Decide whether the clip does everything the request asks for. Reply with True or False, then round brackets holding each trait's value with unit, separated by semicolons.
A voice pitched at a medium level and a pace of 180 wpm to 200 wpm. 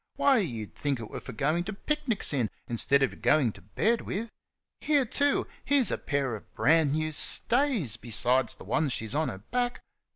True (155 Hz; 190 wpm)